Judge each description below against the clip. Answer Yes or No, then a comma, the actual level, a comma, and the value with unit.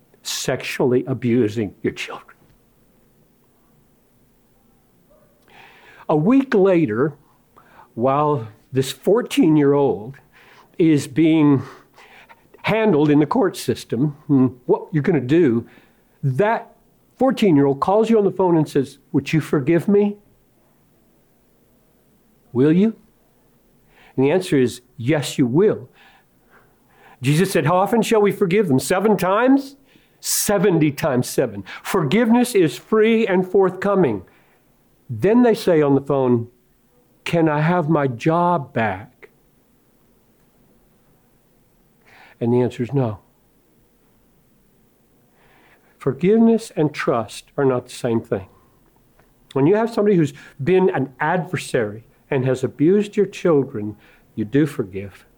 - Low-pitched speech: No, medium, 150 Hz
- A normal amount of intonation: No, wide, 7.3 semitones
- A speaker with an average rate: No, slow, 115 wpm